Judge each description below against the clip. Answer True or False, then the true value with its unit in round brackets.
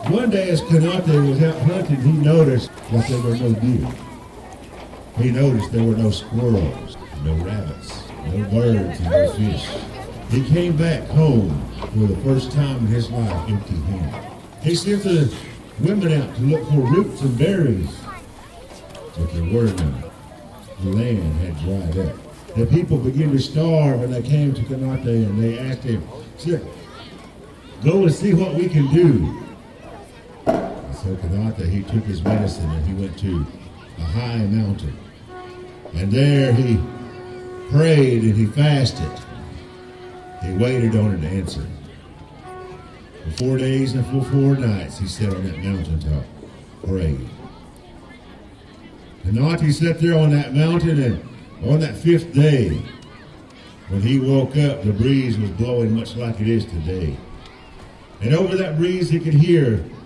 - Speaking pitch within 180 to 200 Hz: False (120 Hz)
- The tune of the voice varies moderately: False (6.6 semitones)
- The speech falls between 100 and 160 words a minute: True (150 wpm)